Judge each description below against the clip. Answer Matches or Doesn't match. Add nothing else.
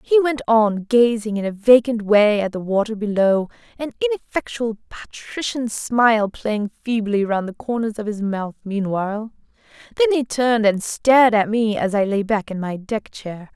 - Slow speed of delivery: Doesn't match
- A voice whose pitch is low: Doesn't match